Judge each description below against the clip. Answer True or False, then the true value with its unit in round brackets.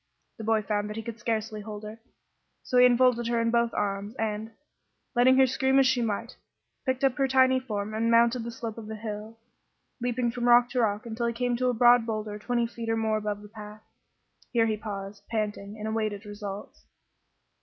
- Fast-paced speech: True (210 wpm)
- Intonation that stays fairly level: True (2.3 semitones)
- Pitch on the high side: True (225 Hz)